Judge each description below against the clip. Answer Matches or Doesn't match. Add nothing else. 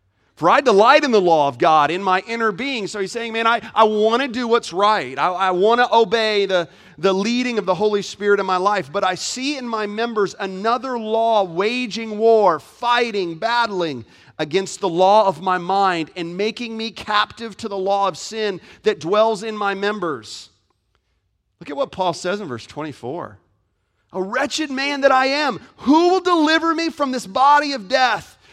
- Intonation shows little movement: Doesn't match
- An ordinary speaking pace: Matches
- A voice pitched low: Doesn't match